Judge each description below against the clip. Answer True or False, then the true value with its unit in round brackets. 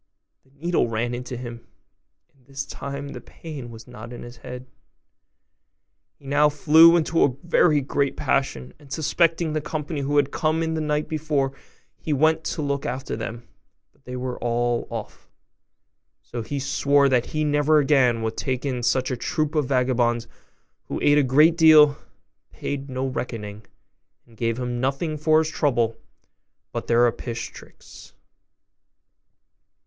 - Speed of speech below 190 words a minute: True (160 wpm)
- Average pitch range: True (3.8 semitones)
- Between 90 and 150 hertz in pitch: True (140 Hz)